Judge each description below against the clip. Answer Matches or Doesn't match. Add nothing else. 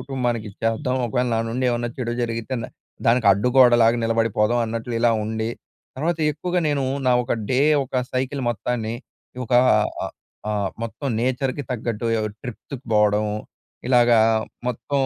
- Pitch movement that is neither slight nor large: Doesn't match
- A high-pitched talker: Doesn't match